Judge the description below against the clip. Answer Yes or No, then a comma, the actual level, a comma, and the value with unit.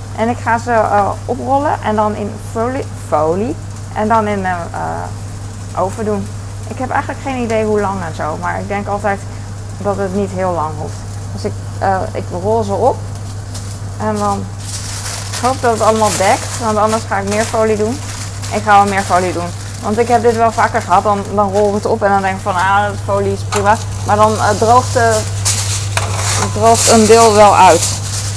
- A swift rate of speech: Yes, fast, 205 wpm